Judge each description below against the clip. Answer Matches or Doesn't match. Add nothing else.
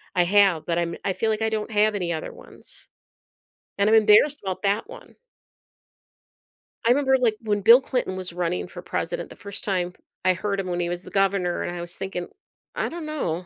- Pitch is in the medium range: Doesn't match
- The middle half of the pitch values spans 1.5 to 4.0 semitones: Matches